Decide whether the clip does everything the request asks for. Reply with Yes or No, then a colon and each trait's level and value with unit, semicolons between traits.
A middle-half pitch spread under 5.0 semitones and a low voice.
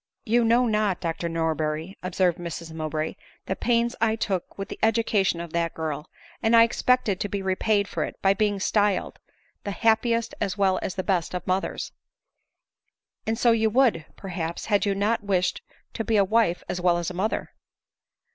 No: average, 4.3 semitones; high, 195 Hz